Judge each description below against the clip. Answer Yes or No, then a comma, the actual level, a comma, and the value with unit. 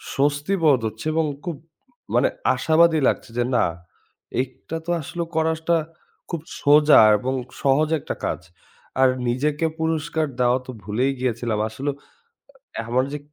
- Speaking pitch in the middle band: Yes, medium, 145 Hz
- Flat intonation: No, average, 3.9 semitones